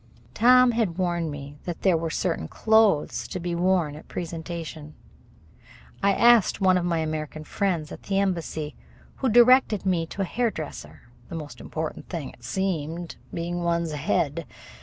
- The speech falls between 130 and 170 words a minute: Yes, average, 160 wpm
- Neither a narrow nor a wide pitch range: Yes, average, 3.7 semitones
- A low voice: No, medium, 170 Hz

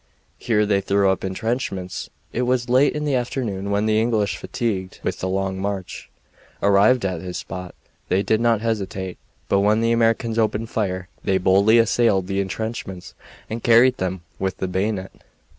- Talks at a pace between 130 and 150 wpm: No, average, 170 wpm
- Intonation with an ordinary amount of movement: Yes, average, 3.3 semitones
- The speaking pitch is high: No, low, 100 Hz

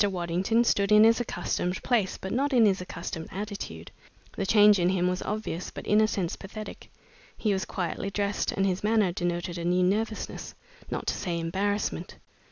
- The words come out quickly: No, average, 180 wpm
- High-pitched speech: Yes, high, 195 Hz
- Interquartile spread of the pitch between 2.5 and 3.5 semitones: Yes, average, 2.9 semitones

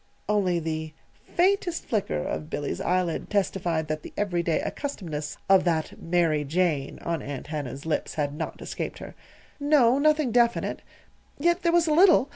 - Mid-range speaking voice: Yes, medium, 175 Hz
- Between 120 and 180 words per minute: Yes, average, 155 wpm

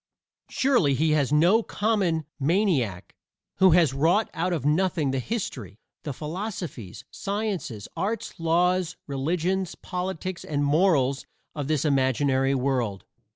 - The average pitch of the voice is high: No, medium, 160 Hz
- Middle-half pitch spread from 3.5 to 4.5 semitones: No, average, 5.3 semitones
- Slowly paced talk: Yes, slow, 120 wpm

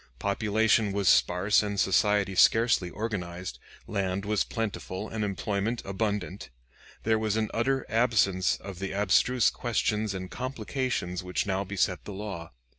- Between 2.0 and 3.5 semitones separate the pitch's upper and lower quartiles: Yes, average, 2.7 semitones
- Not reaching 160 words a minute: Yes, slow, 135 wpm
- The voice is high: No, low, 100 Hz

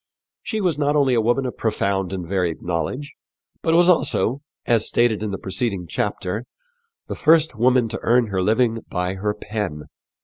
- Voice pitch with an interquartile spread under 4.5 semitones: No, average, 5.1 semitones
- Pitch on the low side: Yes, low, 110 Hz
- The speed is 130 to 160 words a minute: No, average, 175 wpm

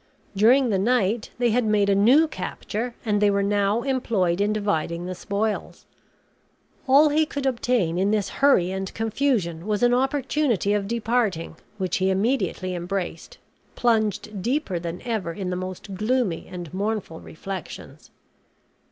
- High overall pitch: Yes, high, 210 Hz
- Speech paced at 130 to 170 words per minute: Yes, average, 150 wpm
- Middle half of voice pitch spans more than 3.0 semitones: Yes, average, 4.4 semitones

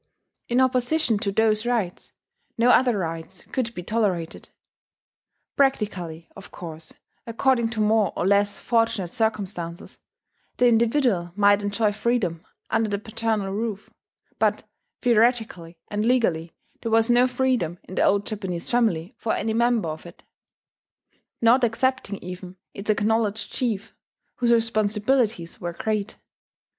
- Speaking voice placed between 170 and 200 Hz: No, high, 215 Hz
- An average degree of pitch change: Yes, average, 3.7 semitones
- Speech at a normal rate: No, slow, 130 wpm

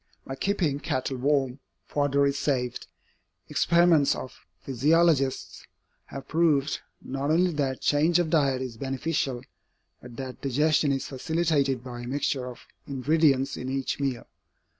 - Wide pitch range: No, average, 2.8 semitones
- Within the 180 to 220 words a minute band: No, slow, 135 wpm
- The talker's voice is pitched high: No, medium, 140 Hz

